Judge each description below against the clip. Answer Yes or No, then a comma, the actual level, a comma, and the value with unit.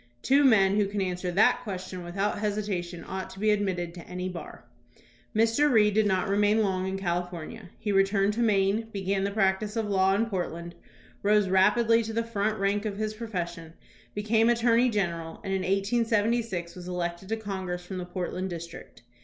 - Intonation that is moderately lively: Yes, average, 3.0 semitones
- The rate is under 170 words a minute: No, average, 195 wpm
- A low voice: No, high, 195 Hz